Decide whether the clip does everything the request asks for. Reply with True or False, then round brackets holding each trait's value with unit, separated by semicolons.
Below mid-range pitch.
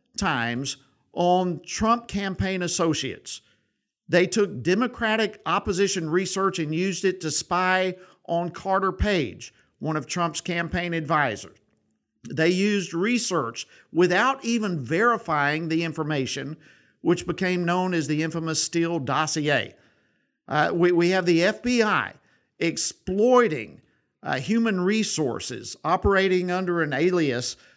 False (175 Hz)